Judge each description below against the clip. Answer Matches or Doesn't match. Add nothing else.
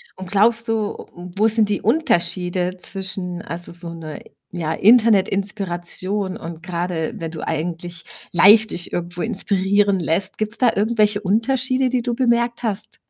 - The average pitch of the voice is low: Doesn't match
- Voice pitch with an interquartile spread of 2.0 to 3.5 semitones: Doesn't match